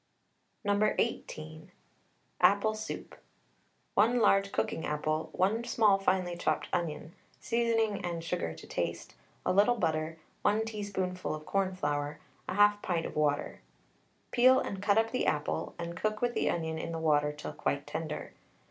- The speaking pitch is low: No, medium, 185 Hz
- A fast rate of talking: No, average, 150 wpm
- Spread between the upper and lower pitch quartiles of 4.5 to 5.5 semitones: Yes, average, 5.0 semitones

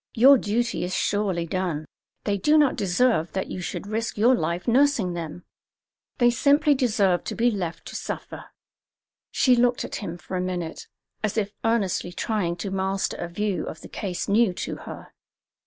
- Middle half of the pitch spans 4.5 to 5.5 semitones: Yes, average, 4.9 semitones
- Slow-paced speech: No, average, 175 wpm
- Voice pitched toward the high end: Yes, high, 200 Hz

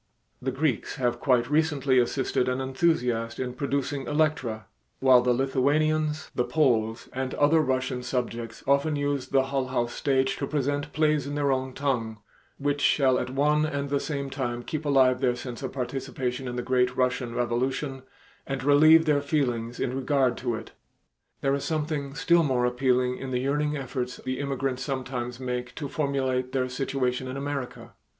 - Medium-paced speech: Yes, average, 170 wpm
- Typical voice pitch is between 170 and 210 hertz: No, low, 135 Hz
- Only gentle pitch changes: Yes, narrow, 2.2 semitones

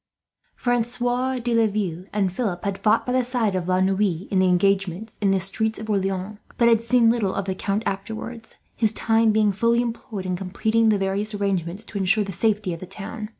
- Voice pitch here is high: Yes, high, 210 Hz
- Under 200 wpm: No, fast, 205 wpm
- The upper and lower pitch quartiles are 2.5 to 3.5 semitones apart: Yes, average, 2.9 semitones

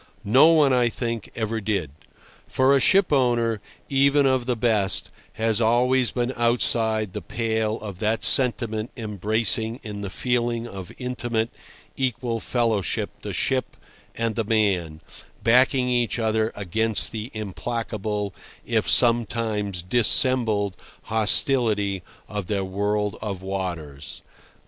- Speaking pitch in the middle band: No, low, 110 Hz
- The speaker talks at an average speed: No, slow, 125 wpm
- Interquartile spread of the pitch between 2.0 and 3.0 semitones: Yes, average, 2.7 semitones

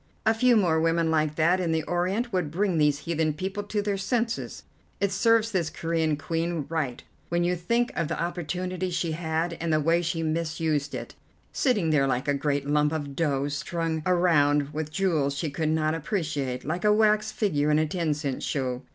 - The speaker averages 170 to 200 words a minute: Yes, average, 195 wpm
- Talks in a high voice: No, medium, 165 Hz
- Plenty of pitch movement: No, average, 3.4 semitones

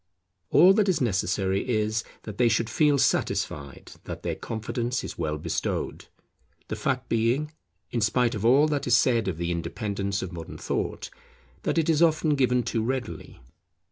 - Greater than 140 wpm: Yes, average, 170 wpm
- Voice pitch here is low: Yes, low, 115 Hz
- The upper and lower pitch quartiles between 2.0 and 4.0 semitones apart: No, average, 5.0 semitones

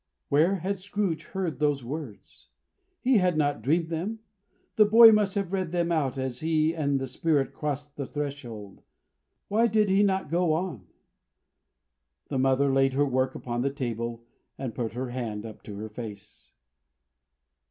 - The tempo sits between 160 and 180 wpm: Yes, average, 165 wpm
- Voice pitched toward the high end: No, medium, 145 Hz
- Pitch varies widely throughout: Yes, wide, 5.9 semitones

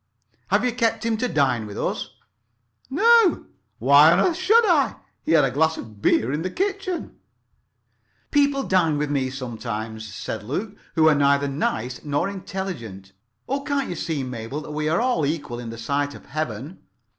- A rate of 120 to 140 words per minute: No, average, 180 wpm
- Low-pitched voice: No, medium, 150 Hz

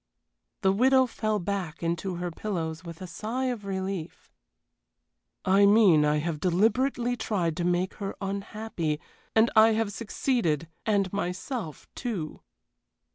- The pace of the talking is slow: Yes, slow, 130 wpm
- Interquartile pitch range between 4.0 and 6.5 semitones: Yes, average, 4.3 semitones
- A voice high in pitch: Yes, high, 195 Hz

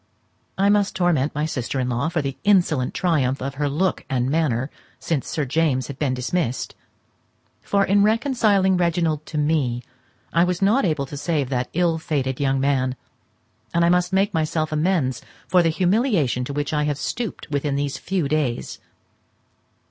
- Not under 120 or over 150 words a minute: No, average, 170 wpm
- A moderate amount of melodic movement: Yes, average, 4.7 semitones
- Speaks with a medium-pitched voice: Yes, medium, 155 Hz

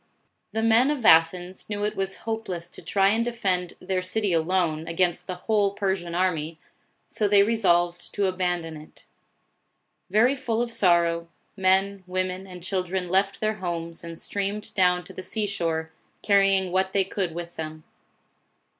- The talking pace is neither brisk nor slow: Yes, average, 165 wpm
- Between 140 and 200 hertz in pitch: Yes, medium, 185 Hz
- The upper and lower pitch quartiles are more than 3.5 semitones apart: No, average, 2.8 semitones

